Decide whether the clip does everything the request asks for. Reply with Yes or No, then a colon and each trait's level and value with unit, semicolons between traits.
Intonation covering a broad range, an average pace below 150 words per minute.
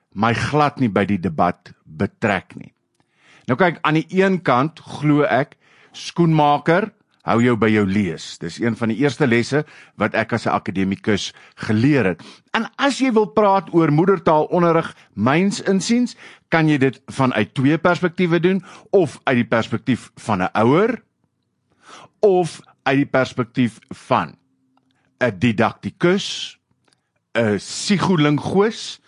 Yes: wide, 7.0 semitones; average, 140 wpm